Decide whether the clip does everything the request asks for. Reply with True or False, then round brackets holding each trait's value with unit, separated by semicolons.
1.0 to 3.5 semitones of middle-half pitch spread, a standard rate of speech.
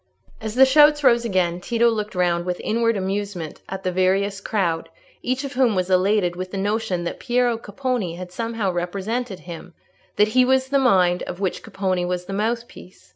False (4.5 semitones; 180 wpm)